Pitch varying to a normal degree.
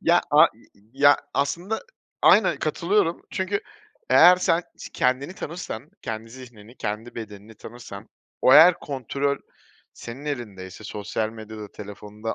Yes: average, 5.0 semitones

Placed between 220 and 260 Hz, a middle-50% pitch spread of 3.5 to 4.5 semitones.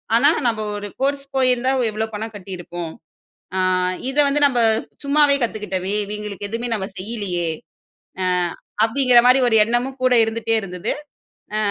Yes: high, 225 Hz; average, 4.1 semitones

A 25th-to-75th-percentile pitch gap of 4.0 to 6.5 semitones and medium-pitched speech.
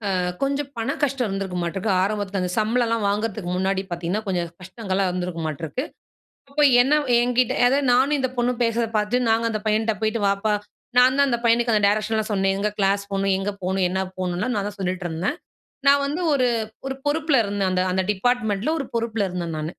No: average, 4.5 semitones; high, 210 Hz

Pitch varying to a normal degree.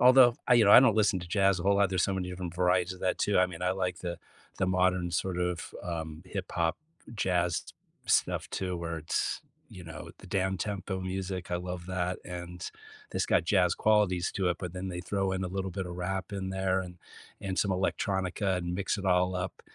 No: narrow, 1.4 semitones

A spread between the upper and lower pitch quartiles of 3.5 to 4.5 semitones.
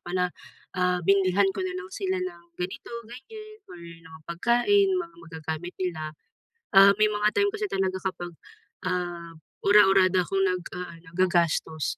Yes: average, 3.9 semitones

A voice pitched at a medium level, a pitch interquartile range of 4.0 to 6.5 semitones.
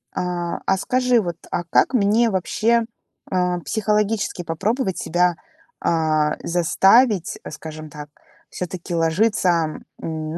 Yes: medium, 180 Hz; average, 4.5 semitones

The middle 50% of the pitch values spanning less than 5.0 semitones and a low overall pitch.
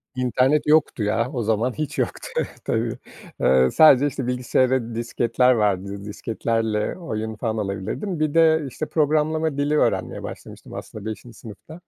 No: wide, 5.4 semitones; low, 125 Hz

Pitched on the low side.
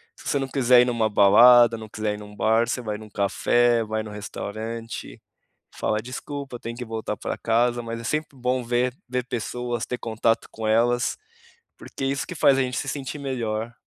Yes: low, 120 Hz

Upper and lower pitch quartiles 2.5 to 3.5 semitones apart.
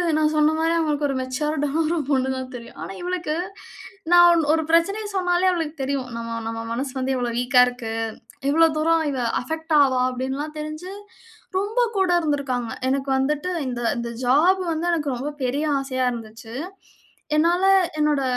No: average, 4.1 semitones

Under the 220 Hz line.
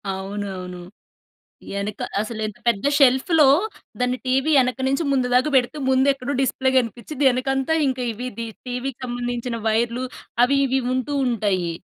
No: very high, 250 Hz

